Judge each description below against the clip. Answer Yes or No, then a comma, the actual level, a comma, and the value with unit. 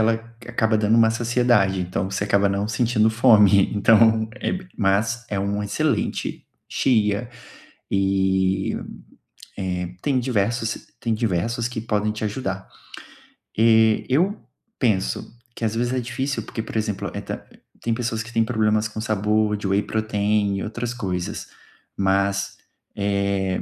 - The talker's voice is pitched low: Yes, low, 110 Hz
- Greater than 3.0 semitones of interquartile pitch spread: No, average, 2.7 semitones